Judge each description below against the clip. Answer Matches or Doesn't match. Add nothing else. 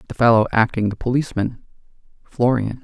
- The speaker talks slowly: Matches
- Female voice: Doesn't match